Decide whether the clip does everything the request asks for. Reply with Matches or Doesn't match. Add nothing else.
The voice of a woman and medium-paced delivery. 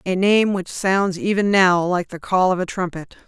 Doesn't match